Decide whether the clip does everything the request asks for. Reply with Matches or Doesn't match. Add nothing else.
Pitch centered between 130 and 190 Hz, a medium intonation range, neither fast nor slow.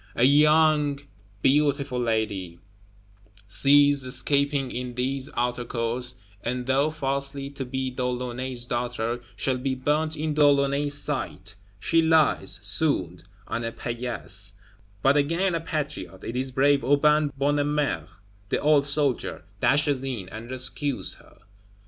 Doesn't match